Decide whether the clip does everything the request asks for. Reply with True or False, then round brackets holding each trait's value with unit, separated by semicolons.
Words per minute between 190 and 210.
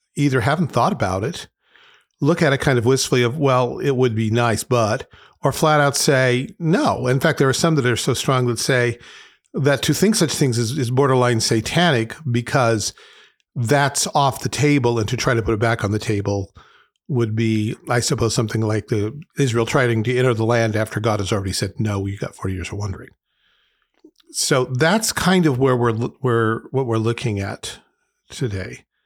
True (200 wpm)